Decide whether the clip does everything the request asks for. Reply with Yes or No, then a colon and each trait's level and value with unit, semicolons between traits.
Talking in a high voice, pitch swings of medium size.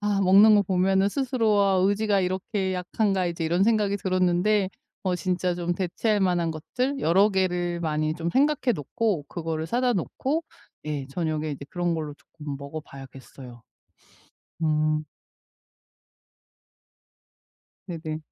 No: medium, 180 Hz; average, 4.4 semitones